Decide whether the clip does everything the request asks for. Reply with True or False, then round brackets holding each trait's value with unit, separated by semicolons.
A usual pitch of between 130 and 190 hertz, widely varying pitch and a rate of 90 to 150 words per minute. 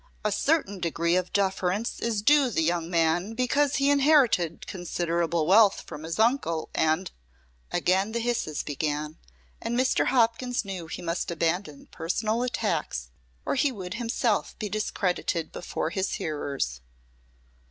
True (185 Hz; 5.9 semitones; 140 wpm)